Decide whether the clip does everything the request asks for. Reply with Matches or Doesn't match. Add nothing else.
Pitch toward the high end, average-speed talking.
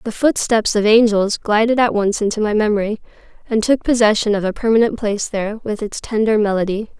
Matches